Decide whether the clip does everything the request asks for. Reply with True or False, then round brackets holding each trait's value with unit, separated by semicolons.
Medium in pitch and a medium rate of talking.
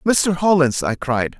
True (150 Hz; 170 wpm)